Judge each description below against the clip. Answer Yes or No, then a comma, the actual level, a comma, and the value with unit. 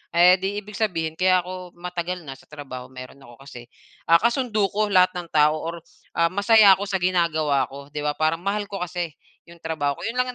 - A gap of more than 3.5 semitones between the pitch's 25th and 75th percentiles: Yes, average, 4.4 semitones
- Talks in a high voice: No, medium, 175 Hz